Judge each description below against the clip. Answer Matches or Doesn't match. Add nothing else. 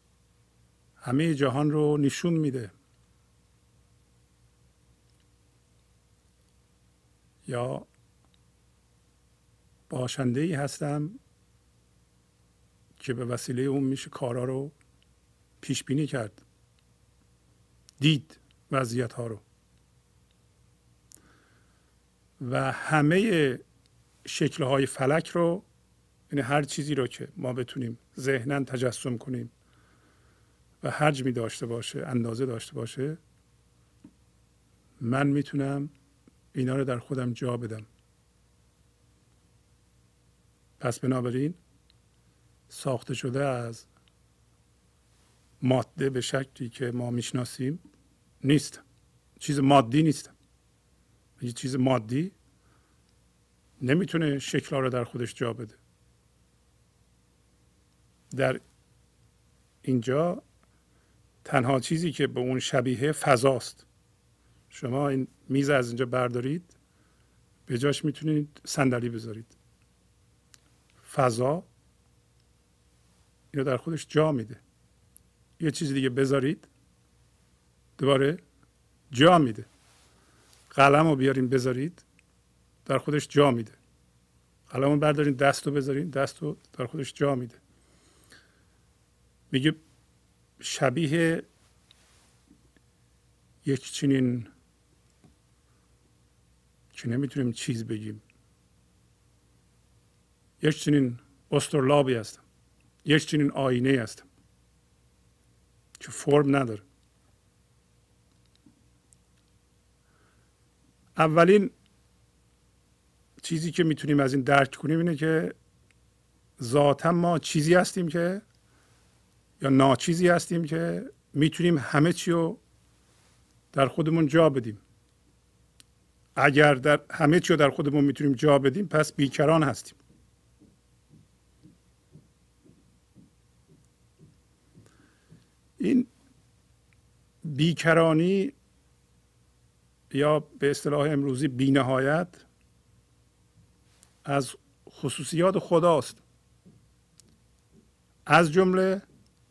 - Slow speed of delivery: Matches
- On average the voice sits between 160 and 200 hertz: Doesn't match